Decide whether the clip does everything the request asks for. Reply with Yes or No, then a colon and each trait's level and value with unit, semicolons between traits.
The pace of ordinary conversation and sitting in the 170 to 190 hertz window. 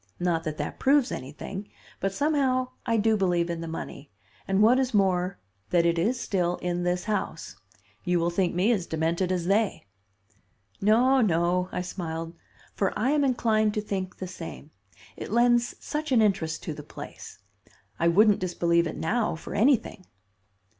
Yes: average, 170 wpm; medium, 185 Hz